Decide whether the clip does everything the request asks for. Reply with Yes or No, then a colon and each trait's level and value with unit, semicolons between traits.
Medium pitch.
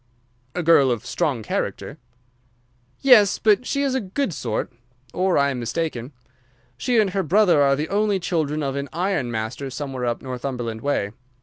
Yes: medium, 145 Hz